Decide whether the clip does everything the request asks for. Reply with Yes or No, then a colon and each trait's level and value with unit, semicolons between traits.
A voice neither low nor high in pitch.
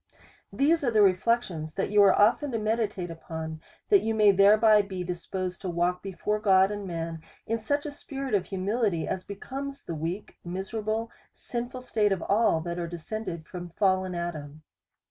No: high, 195 Hz